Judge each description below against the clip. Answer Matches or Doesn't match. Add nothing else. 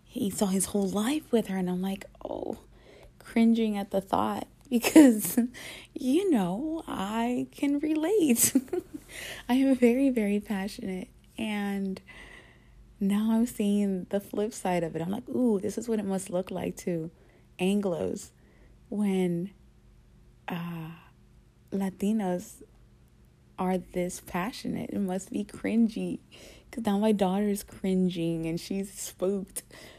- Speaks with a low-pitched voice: Doesn't match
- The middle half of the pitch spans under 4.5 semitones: Matches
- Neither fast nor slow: Doesn't match